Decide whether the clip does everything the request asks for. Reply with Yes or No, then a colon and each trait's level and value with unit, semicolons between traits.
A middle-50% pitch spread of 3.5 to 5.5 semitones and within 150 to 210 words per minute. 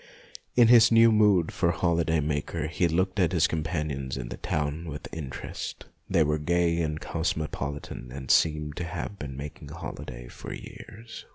No: average, 3.0 semitones; average, 170 wpm